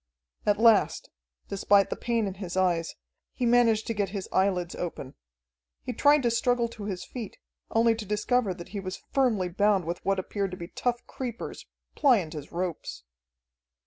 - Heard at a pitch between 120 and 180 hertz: No, high, 205 Hz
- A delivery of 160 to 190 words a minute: Yes, average, 175 wpm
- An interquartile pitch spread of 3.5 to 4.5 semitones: Yes, average, 4.1 semitones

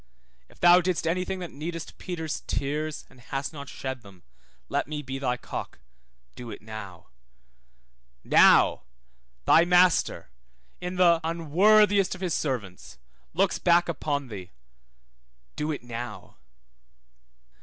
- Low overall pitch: No, medium, 155 Hz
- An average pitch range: No, wide, 5.9 semitones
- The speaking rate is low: Yes, slow, 130 wpm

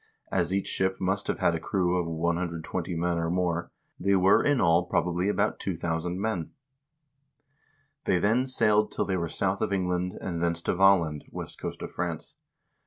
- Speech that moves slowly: No, average, 175 wpm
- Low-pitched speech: Yes, very low, 90 Hz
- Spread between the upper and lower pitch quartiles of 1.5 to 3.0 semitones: Yes, narrow, 2.4 semitones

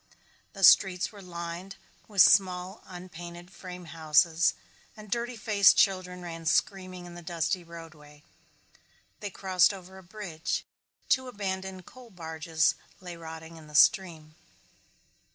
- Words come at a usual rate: No, slow, 130 wpm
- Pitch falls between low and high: Yes, medium, 180 Hz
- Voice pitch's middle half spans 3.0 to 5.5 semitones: No, narrow, 2.6 semitones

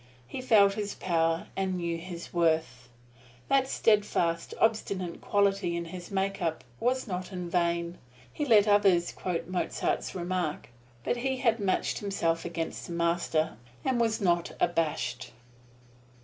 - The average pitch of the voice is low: No, medium, 180 Hz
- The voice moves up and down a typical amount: Yes, average, 3.3 semitones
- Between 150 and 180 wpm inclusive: No, average, 140 wpm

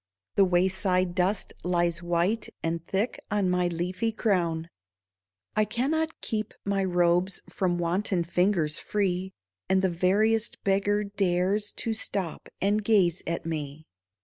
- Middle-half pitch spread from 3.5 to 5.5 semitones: No, average, 2.9 semitones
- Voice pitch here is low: No, medium, 185 Hz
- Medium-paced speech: No, slow, 130 wpm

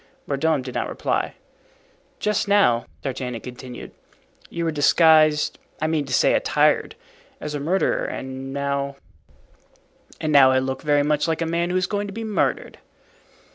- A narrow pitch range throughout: No, average, 3.8 semitones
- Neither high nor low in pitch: Yes, medium, 150 Hz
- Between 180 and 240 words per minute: No, average, 150 wpm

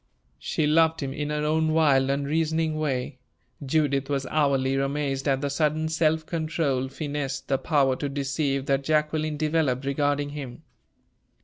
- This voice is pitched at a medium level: Yes, medium, 145 Hz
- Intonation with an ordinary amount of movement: No, narrow, 2.3 semitones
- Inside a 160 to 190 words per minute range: No, average, 145 wpm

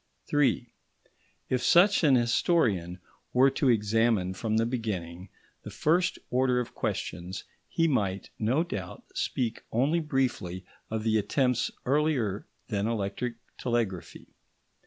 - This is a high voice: No, low, 115 Hz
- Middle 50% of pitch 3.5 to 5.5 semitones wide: Yes, average, 4.9 semitones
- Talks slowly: Yes, slow, 125 wpm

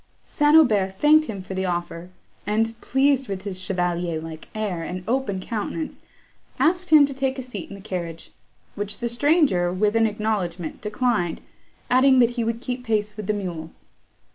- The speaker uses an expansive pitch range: Yes, wide, 5.7 semitones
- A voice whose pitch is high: Yes, high, 210 Hz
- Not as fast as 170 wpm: No, average, 175 wpm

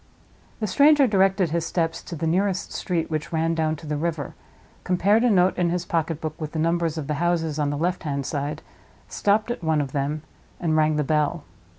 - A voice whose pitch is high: No, medium, 165 Hz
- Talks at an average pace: No, fast, 210 wpm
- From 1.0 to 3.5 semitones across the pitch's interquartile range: Yes, average, 2.7 semitones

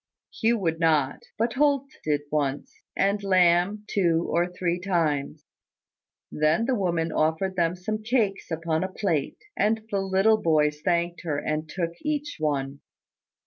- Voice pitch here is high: No, medium, 175 Hz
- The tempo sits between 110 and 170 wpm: Yes, average, 145 wpm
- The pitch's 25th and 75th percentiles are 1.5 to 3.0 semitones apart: No, average, 4.3 semitones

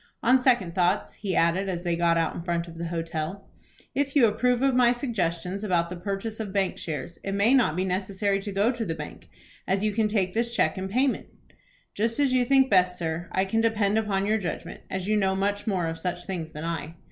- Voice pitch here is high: Yes, high, 195 Hz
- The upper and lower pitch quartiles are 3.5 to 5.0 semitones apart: Yes, average, 4.4 semitones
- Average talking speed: No, fast, 230 wpm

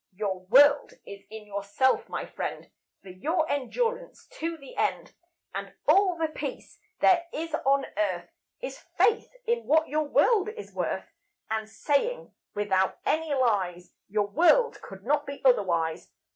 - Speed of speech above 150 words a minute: No, average, 145 wpm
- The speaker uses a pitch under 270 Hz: No, very high, 275 Hz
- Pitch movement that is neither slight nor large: No, wide, 8.4 semitones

